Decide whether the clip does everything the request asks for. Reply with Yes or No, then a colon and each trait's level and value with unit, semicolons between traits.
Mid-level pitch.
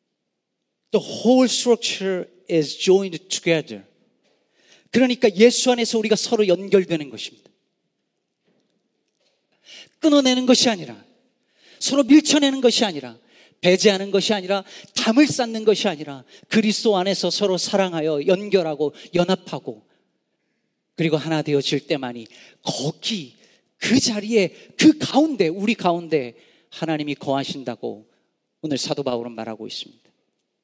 No: high, 195 Hz